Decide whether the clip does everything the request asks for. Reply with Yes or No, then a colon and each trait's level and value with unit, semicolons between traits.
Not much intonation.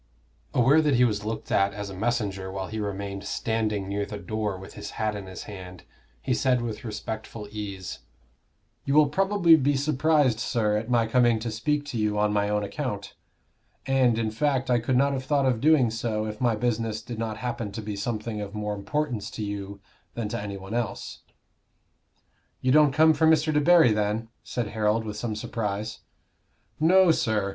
No: average, 3.9 semitones